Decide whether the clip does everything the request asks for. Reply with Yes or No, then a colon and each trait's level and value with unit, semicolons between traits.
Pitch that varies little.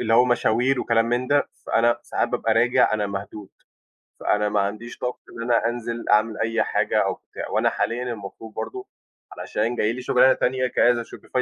Yes: narrow, 2.1 semitones